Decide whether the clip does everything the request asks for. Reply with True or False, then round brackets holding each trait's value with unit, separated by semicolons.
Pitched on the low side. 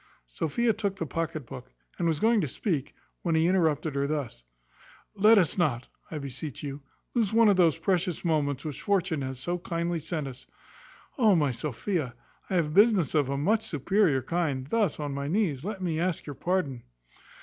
False (160 Hz)